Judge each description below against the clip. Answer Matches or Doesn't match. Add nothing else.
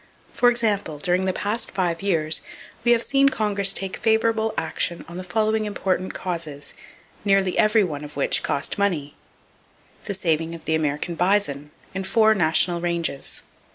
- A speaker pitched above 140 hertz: Matches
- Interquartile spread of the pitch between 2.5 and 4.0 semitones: Doesn't match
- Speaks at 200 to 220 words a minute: Doesn't match